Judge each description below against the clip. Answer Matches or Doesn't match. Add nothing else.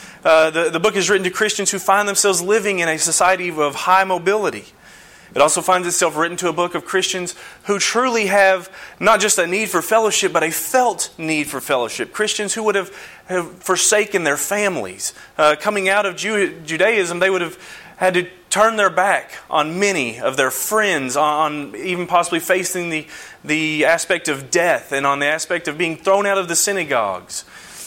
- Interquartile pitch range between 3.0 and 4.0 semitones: Matches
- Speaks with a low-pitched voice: Doesn't match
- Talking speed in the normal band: Matches